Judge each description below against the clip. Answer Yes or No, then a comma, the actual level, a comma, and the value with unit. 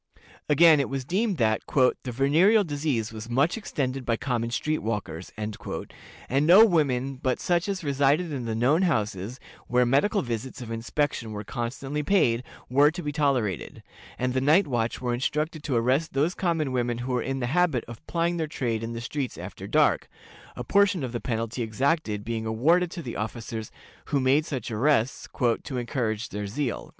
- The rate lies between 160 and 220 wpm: Yes, average, 180 wpm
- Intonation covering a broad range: No, average, 4.6 semitones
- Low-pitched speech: Yes, low, 130 Hz